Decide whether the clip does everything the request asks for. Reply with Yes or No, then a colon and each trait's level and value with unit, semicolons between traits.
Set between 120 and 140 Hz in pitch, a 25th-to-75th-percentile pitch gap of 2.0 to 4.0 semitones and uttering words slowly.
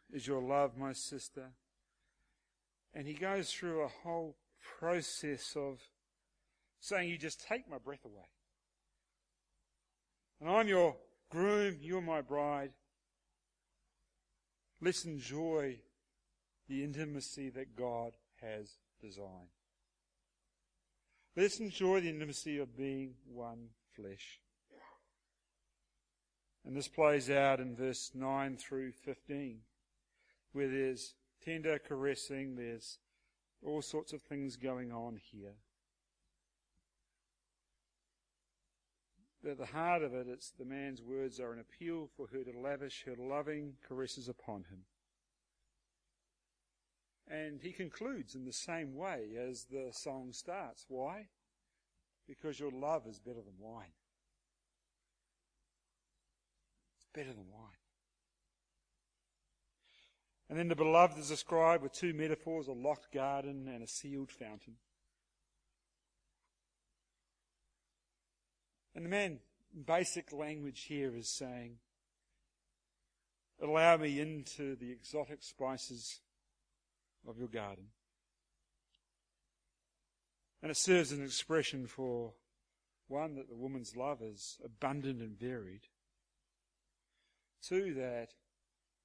No: low, 135 Hz; average, 4.4 semitones; slow, 110 wpm